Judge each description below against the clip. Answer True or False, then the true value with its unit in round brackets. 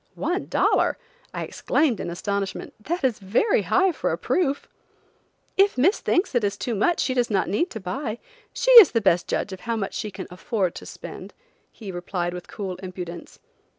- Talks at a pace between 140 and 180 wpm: False (190 wpm)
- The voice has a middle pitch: False (215 Hz)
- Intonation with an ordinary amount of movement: False (7.9 semitones)